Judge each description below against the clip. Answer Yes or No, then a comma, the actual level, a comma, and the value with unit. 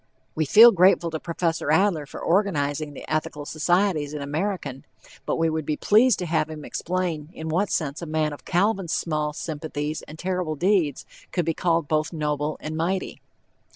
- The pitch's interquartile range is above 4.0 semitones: No, average, 3.1 semitones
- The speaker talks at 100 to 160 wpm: No, average, 180 wpm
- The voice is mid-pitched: Yes, medium, 160 Hz